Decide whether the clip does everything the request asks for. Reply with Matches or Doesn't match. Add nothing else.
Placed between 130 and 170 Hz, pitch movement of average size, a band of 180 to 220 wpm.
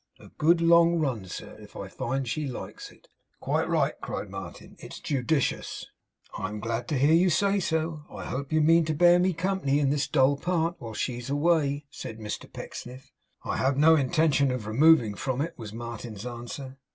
Matches